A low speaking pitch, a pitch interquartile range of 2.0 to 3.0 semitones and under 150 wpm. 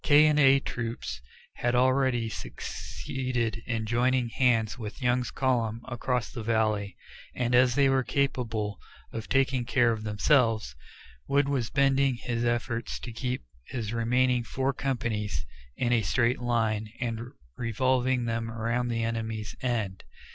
Yes: low, 120 Hz; narrow, 2.4 semitones; average, 140 wpm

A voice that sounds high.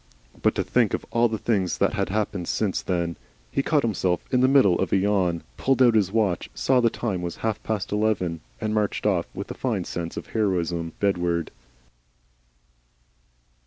No: low, 100 Hz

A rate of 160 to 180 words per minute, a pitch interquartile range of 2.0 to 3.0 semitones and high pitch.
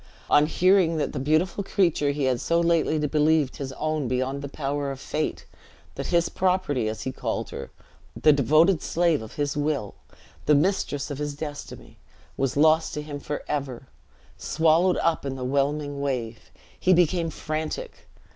No: average, 165 wpm; average, 2.7 semitones; medium, 150 Hz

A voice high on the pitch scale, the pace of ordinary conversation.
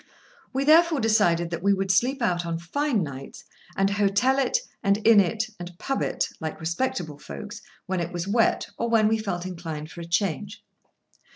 Yes: high, 195 Hz; average, 185 wpm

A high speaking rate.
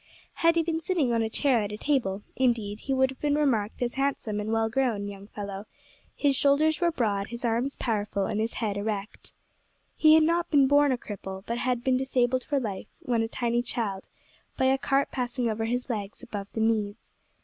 Yes: fast, 215 wpm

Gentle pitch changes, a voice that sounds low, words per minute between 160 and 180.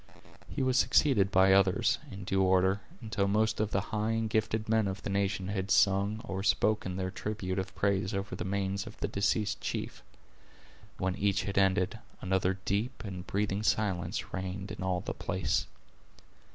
Yes: narrow, 1.8 semitones; low, 100 Hz; average, 175 wpm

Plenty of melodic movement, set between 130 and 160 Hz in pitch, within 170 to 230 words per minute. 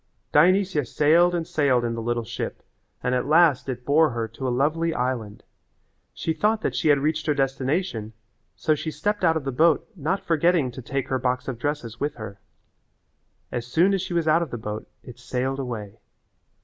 No: average, 4.7 semitones; medium, 140 Hz; average, 200 wpm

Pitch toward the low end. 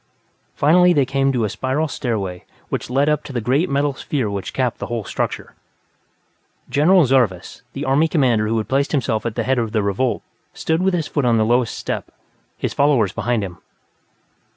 Yes: low, 130 Hz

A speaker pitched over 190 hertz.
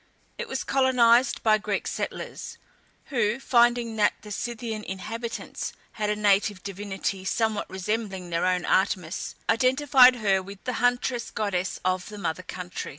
Yes: high, 210 Hz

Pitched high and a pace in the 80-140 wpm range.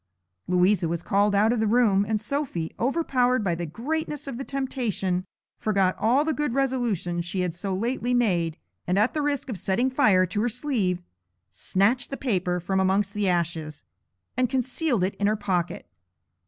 No: high, 210 Hz; average, 180 wpm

